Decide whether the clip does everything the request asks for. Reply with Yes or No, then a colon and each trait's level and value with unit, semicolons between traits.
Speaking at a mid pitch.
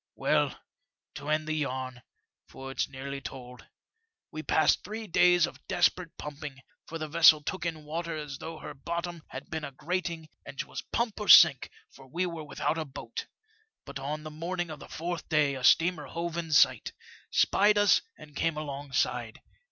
Yes: medium, 155 Hz